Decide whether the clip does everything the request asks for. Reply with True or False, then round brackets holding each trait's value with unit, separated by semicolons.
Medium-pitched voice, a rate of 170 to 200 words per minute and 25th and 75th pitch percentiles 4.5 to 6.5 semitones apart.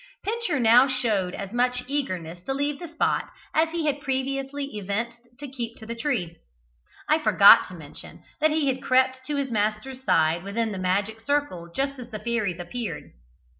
False (250 Hz; 180 wpm; 4.9 semitones)